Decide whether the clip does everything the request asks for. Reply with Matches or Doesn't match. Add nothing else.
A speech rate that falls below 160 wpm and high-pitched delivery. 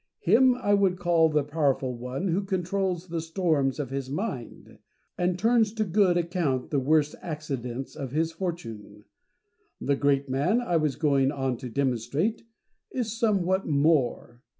Doesn't match